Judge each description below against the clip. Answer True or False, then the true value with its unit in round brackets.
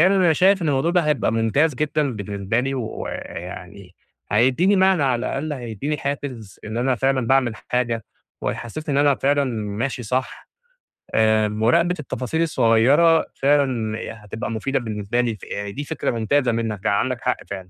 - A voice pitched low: True (125 Hz)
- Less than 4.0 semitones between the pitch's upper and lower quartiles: False (4.7 semitones)